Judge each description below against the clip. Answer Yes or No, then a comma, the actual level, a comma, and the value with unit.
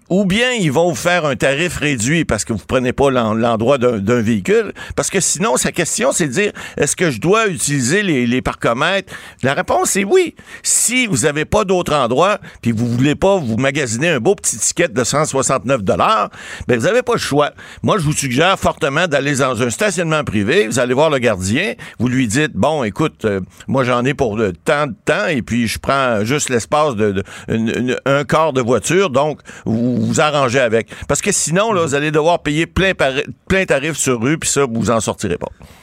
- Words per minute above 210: Yes, fast, 220 wpm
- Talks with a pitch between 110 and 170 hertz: Yes, medium, 140 Hz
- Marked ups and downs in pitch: Yes, wide, 6.0 semitones